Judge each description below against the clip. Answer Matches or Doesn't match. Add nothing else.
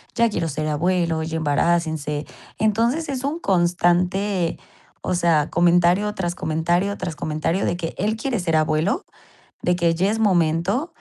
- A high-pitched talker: Doesn't match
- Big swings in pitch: Doesn't match